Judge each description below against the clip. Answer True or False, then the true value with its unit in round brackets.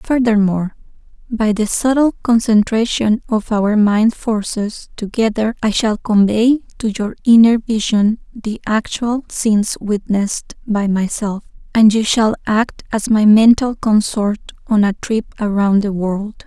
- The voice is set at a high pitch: True (215 Hz)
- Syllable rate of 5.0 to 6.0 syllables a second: False (4.1 syllables/s)